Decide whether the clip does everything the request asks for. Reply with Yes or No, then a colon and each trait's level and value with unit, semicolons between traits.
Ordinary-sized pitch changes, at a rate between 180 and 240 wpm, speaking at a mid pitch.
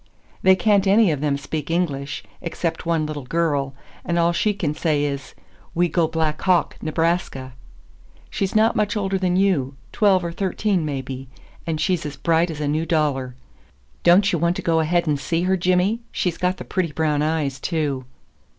Yes: average, 3.7 semitones; average, 185 wpm; medium, 165 Hz